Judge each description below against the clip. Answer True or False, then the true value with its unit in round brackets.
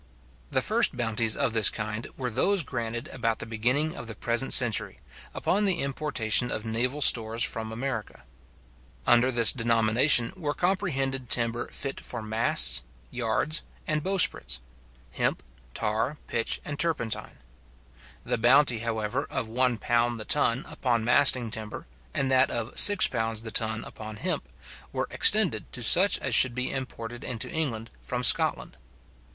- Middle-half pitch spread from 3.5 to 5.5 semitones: False (3.1 semitones)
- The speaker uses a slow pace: False (145 wpm)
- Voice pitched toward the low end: True (120 Hz)